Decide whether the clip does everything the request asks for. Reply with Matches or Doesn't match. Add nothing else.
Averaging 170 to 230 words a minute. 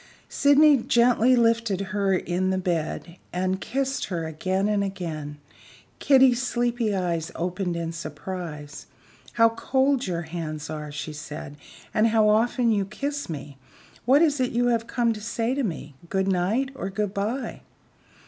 Doesn't match